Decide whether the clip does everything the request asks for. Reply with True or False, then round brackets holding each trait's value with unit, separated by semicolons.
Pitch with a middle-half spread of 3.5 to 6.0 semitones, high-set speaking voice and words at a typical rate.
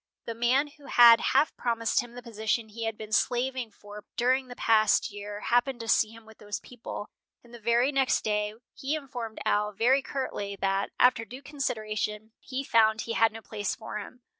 False (2.7 semitones; 230 Hz; 195 wpm)